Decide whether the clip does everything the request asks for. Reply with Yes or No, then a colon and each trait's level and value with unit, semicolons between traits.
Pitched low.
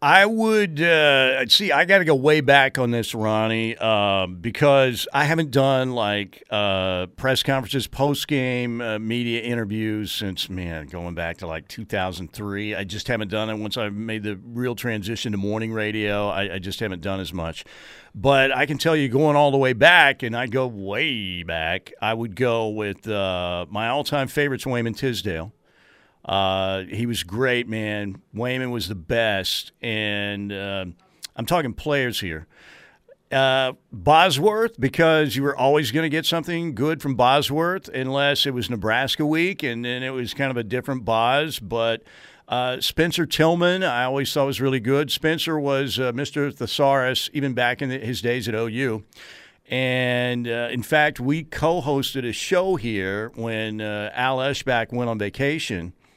Yes: low, 120 Hz